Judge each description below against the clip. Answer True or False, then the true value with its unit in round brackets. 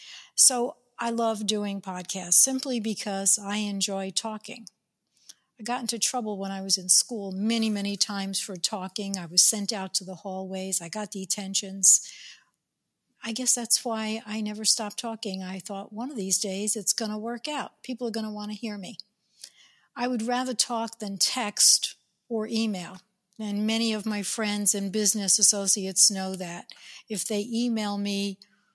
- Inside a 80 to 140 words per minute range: False (175 wpm)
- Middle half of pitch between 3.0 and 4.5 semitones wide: False (2.5 semitones)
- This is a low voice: False (210 Hz)